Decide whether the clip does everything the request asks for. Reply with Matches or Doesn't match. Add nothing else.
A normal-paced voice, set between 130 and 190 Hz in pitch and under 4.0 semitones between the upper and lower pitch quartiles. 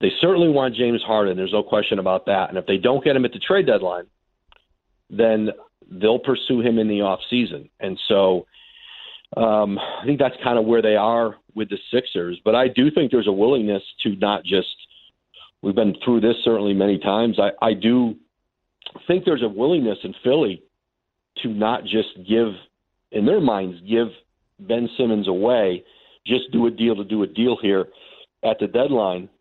Doesn't match